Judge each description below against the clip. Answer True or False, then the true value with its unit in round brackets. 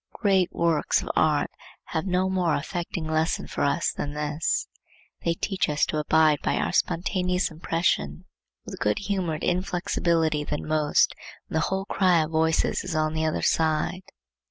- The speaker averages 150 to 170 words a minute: True (160 wpm)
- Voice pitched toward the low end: False (160 Hz)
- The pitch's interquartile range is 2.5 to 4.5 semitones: True (2.8 semitones)